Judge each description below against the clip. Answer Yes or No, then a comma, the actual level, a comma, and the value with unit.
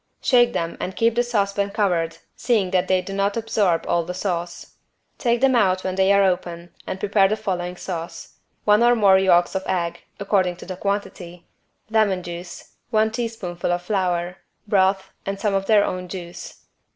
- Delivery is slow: No, average, 185 wpm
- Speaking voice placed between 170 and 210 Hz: Yes, high, 190 Hz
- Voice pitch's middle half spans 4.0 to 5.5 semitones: No, average, 2.8 semitones